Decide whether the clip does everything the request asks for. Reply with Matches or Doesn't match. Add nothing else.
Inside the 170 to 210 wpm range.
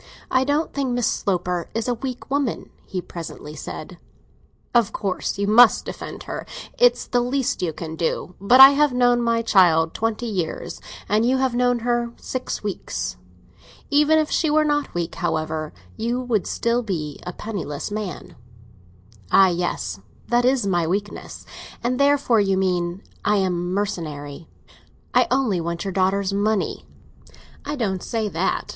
Doesn't match